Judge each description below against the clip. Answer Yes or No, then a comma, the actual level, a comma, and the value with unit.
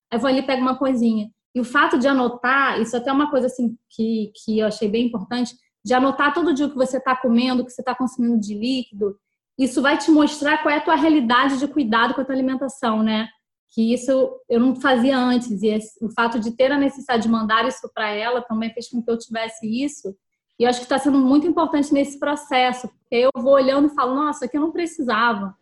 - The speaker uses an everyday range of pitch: Yes, average, 3.0 semitones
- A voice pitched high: Yes, very high, 250 Hz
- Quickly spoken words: Yes, fast, 240 wpm